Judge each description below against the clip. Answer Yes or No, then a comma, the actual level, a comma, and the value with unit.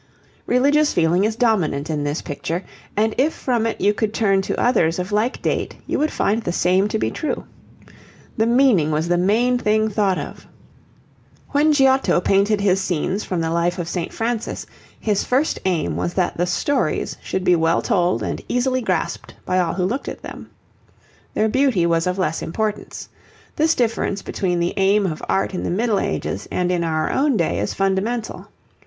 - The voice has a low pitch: No, high, 195 Hz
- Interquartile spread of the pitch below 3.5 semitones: No, average, 4.8 semitones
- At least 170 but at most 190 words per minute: Yes, average, 185 wpm